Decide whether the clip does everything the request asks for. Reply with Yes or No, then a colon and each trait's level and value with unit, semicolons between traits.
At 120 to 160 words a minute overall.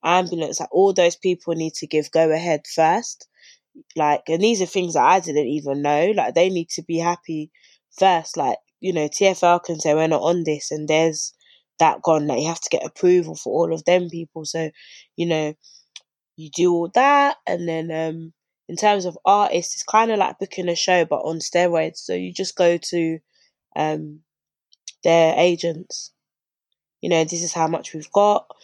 No: average, 195 wpm